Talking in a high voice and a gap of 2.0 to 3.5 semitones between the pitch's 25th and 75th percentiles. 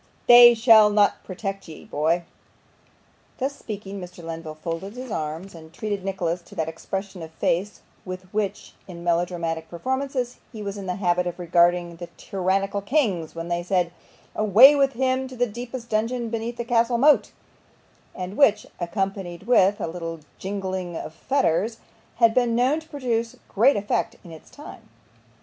No: high, 195 Hz; average, 5.3 semitones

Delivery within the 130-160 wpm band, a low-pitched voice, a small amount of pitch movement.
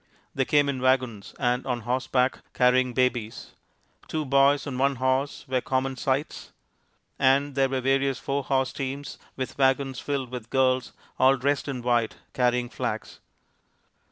Yes: average, 150 wpm; low, 130 Hz; narrow, 1.5 semitones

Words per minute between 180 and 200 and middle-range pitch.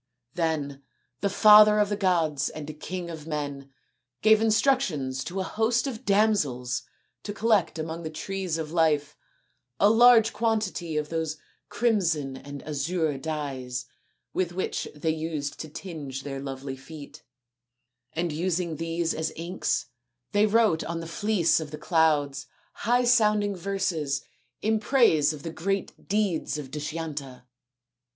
No: average, 140 wpm; medium, 165 Hz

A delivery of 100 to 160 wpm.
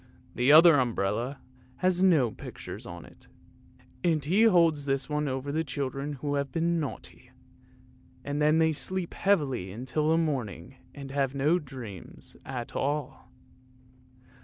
Yes: average, 140 wpm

